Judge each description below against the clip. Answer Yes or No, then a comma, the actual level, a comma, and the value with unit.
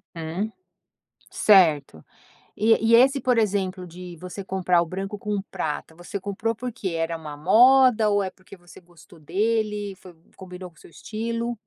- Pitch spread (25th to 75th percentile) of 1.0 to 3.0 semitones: No, average, 3.8 semitones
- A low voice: No, high, 190 Hz